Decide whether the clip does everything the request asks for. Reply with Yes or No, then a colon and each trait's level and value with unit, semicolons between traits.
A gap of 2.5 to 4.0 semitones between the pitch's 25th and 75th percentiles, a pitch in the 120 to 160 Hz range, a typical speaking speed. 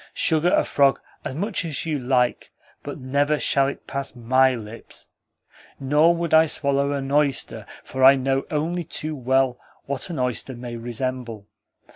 Yes: average, 2.8 semitones; low, 135 Hz; average, 160 wpm